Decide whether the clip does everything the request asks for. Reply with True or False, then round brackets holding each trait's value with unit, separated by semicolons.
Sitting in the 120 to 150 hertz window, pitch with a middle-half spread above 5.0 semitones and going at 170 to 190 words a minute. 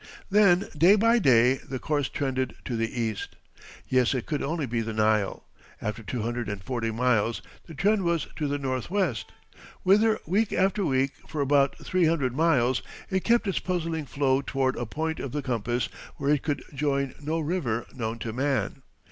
True (140 Hz; 5.4 semitones; 180 wpm)